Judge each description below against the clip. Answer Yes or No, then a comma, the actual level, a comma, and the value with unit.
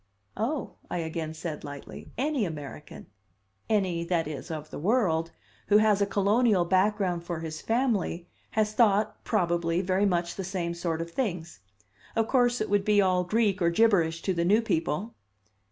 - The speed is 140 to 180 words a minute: Yes, average, 170 wpm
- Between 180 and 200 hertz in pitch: Yes, medium, 185 Hz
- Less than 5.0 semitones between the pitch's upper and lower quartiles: Yes, average, 4.2 semitones